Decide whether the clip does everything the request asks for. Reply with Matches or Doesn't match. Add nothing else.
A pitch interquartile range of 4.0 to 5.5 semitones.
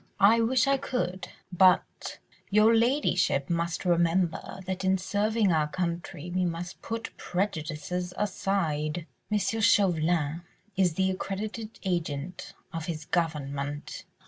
Doesn't match